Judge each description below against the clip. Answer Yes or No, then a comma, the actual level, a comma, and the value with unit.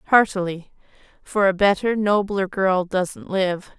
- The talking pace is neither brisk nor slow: No, slow, 125 wpm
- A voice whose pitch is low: No, high, 195 Hz